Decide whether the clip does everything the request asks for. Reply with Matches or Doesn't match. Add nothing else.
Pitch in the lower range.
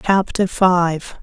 Doesn't match